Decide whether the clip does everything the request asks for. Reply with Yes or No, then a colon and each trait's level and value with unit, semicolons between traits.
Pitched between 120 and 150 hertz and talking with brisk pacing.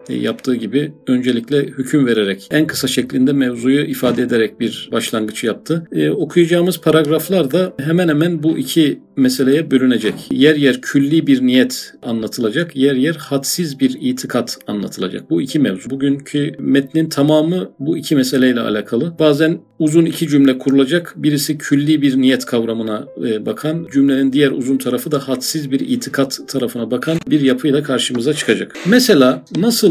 Yes: medium, 140 Hz; fast, 145 wpm